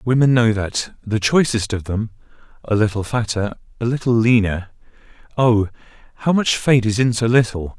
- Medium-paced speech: Yes, average, 160 wpm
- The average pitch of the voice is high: No, low, 115 Hz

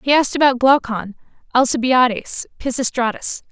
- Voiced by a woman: Yes, female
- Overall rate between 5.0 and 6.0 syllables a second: Yes, 5.3 syllables/s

